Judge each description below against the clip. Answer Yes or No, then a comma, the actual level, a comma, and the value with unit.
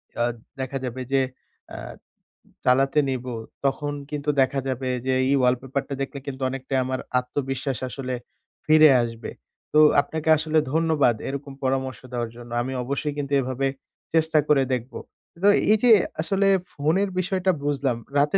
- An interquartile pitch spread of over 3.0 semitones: No, narrow, 2.6 semitones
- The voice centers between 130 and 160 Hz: Yes, low, 135 Hz